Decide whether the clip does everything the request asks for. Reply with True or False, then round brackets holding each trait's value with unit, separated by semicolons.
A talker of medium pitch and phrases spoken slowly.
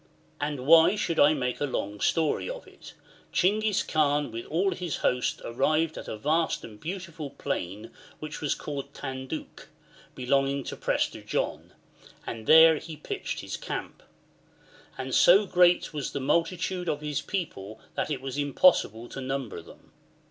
False (145 Hz; 155 wpm)